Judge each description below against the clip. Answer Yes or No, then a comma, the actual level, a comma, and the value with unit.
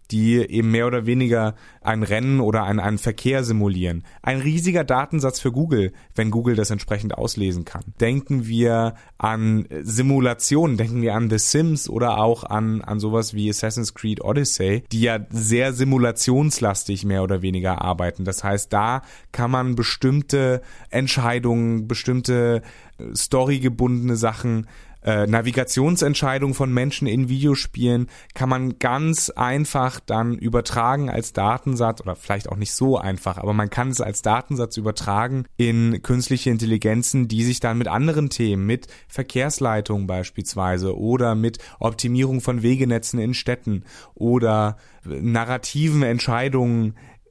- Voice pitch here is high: No, low, 115 Hz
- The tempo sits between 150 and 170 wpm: No, average, 135 wpm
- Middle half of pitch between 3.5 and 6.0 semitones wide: No, average, 3.1 semitones